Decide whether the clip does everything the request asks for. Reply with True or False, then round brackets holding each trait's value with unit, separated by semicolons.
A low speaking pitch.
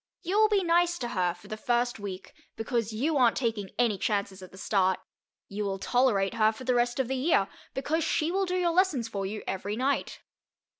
False (235 Hz)